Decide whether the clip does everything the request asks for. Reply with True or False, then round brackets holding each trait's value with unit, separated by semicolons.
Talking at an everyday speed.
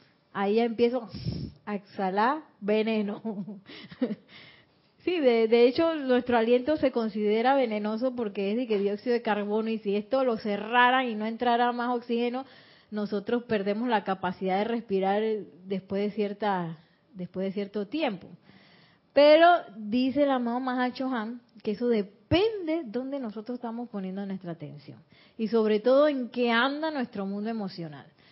True (145 wpm)